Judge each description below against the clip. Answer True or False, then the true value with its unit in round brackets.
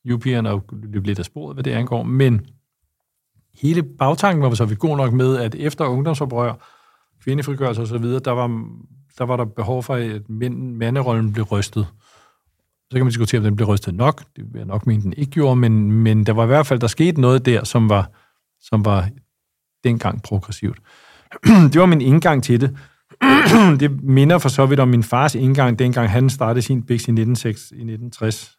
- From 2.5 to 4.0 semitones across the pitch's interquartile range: True (3.4 semitones)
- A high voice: False (125 Hz)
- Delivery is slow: False (185 wpm)